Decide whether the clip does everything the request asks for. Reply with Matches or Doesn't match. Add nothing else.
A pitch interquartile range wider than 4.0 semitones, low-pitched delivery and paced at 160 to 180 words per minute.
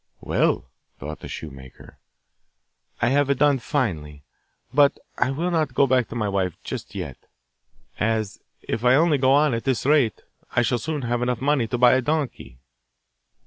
Matches